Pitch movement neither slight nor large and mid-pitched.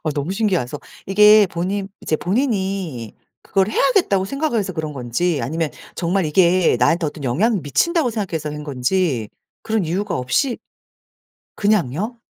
No: wide, 5.7 semitones; medium, 180 Hz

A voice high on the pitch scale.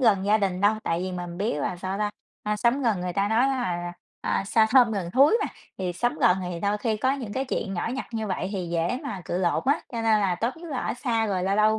Yes: high, 205 Hz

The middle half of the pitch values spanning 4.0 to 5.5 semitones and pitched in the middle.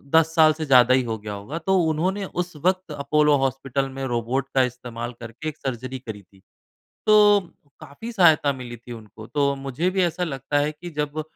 Yes: average, 5.1 semitones; medium, 145 Hz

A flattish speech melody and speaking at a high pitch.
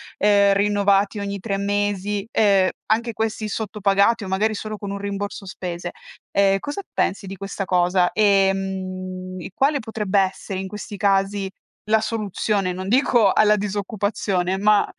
Yes: narrow, 1.6 semitones; high, 200 Hz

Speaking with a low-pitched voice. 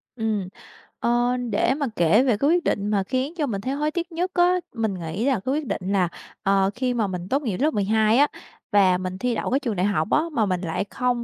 No: high, 225 Hz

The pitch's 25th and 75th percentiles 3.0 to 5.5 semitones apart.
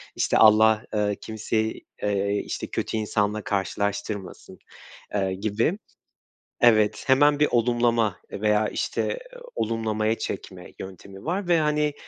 No: narrow, 2.6 semitones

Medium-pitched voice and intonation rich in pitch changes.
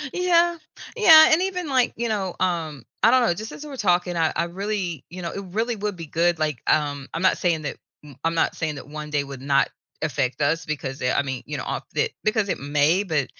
Yes: medium, 170 Hz; wide, 6.5 semitones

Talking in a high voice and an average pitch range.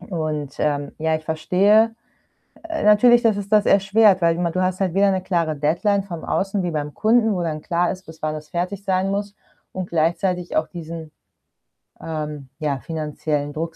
No: medium, 175 Hz; average, 4.0 semitones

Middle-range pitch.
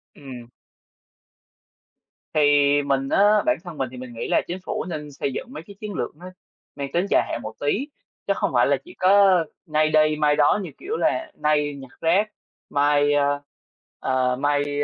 Yes: medium, 150 Hz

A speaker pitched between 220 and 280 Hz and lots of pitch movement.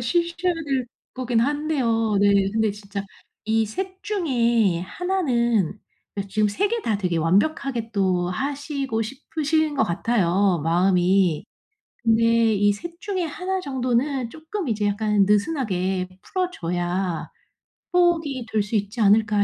Yes: high, 225 Hz; wide, 6.7 semitones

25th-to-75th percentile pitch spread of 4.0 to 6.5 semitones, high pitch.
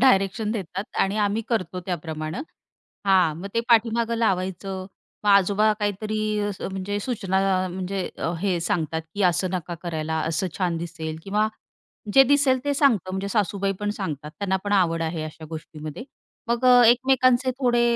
Yes: average, 4.5 semitones; high, 195 Hz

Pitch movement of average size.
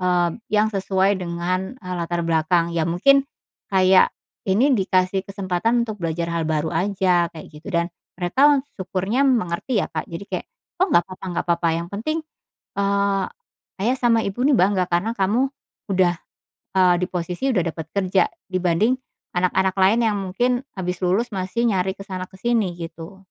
Yes: average, 3.3 semitones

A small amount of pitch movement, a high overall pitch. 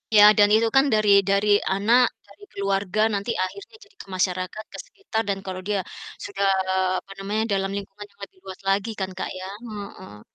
Yes: narrow, 1.7 semitones; high, 200 Hz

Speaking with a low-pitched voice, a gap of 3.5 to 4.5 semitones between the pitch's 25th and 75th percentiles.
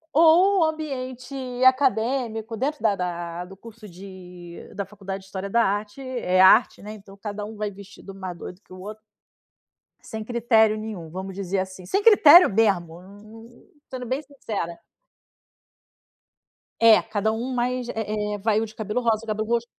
No: high, 215 Hz; average, 3.8 semitones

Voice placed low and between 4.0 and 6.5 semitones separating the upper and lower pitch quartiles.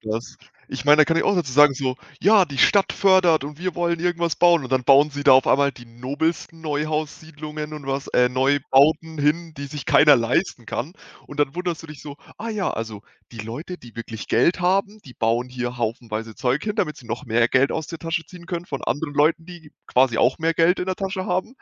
No: medium, 150 Hz; average, 4.7 semitones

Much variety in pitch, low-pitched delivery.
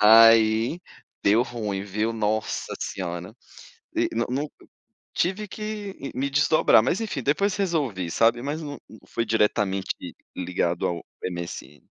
Yes: wide, 6.4 semitones; low, 115 Hz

